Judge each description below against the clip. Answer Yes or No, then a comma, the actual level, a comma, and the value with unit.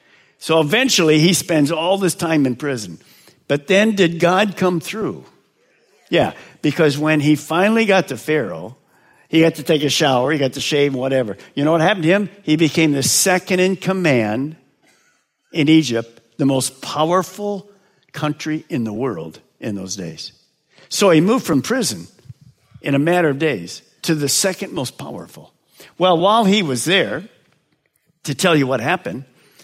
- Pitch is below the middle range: No, medium, 160 Hz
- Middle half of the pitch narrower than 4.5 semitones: No, average, 4.8 semitones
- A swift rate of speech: No, average, 170 wpm